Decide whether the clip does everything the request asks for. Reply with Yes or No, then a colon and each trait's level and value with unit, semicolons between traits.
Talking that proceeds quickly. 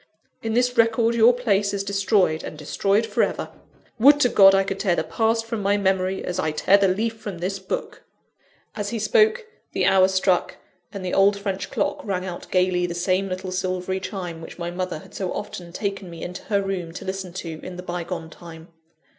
Yes: fast, 210 wpm